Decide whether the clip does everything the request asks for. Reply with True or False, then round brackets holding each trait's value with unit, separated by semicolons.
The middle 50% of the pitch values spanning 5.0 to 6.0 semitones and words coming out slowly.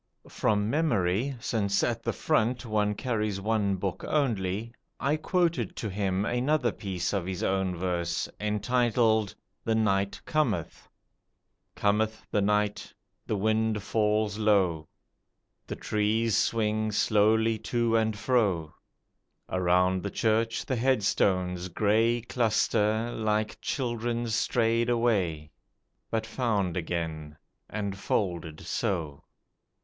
False (3.1 semitones; 115 wpm)